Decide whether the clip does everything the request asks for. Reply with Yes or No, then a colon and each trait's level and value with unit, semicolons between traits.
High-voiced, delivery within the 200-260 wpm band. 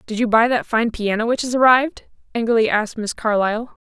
Yes: high, 225 Hz; fast, 205 wpm